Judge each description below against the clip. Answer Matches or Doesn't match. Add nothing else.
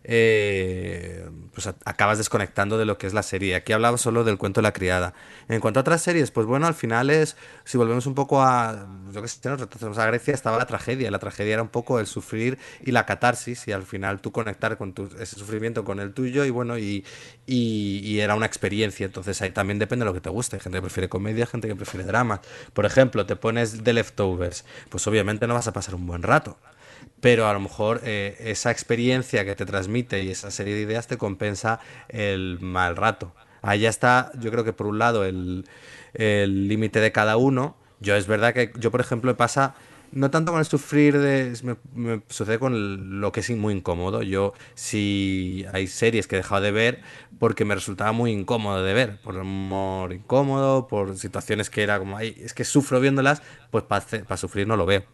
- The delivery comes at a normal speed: Doesn't match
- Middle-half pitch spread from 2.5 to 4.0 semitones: Matches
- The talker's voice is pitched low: Matches